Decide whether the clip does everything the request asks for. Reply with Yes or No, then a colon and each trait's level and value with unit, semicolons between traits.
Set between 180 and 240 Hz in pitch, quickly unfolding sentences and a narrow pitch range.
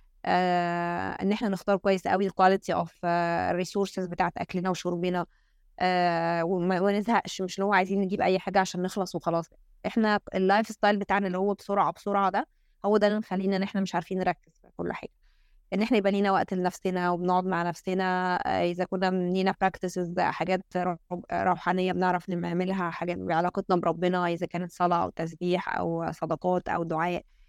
Yes: medium, 185 Hz; fast, 160 wpm; narrow, 1.6 semitones